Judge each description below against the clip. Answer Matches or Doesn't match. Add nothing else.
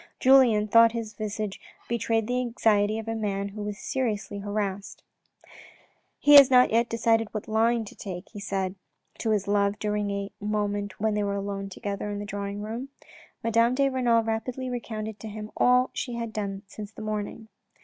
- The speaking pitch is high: Matches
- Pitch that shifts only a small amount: Matches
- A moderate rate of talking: Matches